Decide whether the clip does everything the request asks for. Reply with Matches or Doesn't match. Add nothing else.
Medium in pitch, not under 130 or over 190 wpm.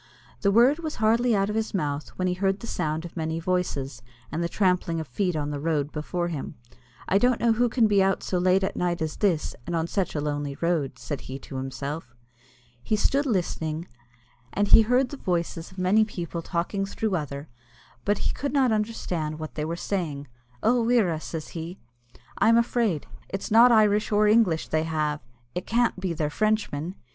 Doesn't match